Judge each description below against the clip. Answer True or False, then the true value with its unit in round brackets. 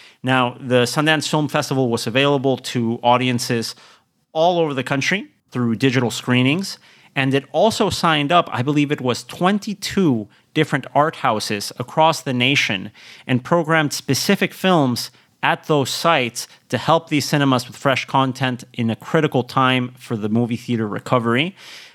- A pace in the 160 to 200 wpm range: False (150 wpm)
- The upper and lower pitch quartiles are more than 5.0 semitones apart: False (4.2 semitones)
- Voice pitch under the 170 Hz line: True (135 Hz)